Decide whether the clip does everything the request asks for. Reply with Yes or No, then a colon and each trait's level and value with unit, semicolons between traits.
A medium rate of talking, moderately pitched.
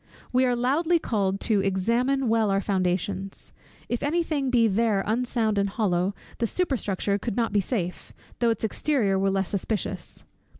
No: average, 170 wpm; high, 220 Hz